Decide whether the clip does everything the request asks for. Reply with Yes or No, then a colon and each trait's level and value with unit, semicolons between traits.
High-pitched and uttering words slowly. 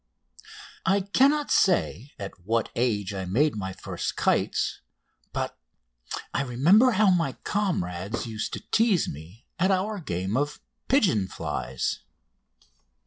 No: low, 135 Hz; slow, 125 wpm